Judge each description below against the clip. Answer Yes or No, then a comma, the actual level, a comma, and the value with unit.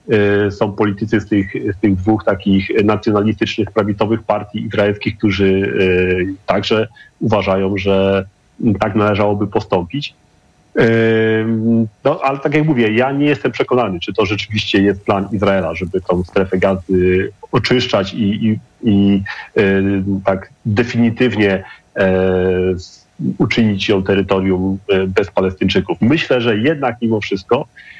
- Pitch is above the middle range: No, low, 105 Hz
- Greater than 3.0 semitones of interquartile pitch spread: No, narrow, 2.5 semitones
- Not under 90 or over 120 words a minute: Yes, average, 115 wpm